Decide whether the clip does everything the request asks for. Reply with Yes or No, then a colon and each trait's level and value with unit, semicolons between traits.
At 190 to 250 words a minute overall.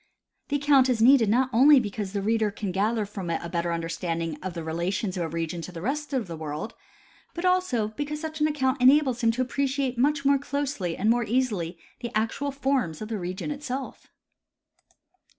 Yes: average, 200 wpm